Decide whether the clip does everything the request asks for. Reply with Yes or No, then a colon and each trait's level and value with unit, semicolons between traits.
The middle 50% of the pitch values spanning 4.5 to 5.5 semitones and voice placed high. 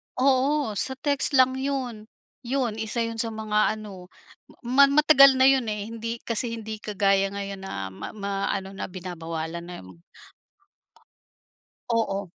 Yes: average, 4.8 semitones; high, 220 Hz